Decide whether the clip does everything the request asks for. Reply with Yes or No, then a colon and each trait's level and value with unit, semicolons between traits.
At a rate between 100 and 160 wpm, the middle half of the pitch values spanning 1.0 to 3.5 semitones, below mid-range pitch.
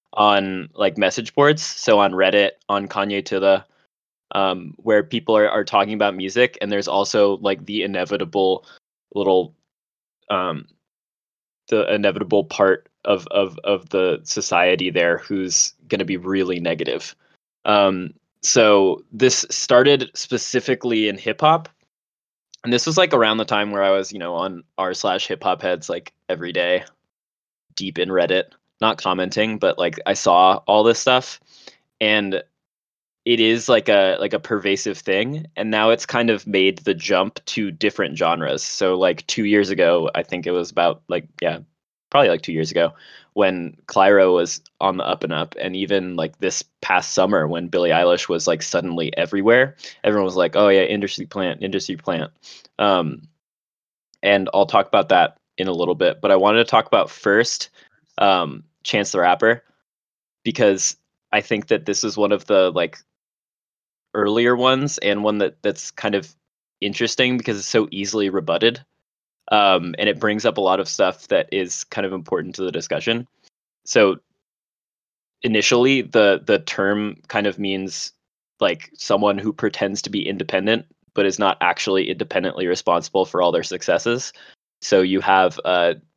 No: average, 170 wpm; average, 2.8 semitones; low, 100 Hz